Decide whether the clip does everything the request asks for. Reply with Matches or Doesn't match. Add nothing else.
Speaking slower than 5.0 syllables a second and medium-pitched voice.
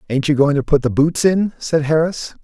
Doesn't match